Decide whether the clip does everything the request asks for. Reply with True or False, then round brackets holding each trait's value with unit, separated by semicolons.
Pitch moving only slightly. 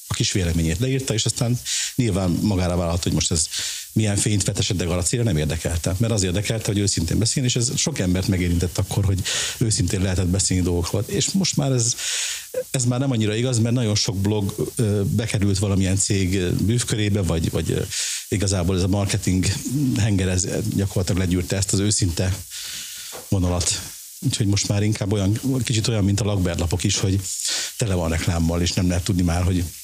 False (3.9 semitones)